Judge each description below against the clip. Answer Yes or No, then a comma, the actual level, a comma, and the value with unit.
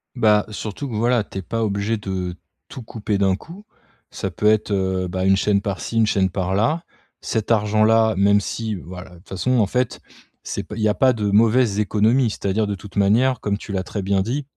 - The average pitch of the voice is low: Yes, low, 105 Hz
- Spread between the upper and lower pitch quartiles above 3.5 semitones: No, average, 2.7 semitones